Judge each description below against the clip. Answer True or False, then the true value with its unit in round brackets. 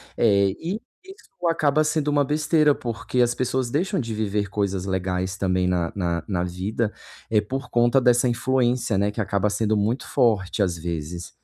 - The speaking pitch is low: True (110 Hz)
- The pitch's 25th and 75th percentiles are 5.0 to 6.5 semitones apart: True (5.6 semitones)